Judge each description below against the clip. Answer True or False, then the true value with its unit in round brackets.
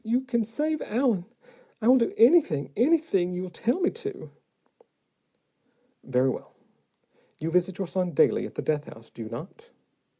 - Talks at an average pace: True (160 wpm)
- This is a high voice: True (210 Hz)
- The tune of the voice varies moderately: False (8.1 semitones)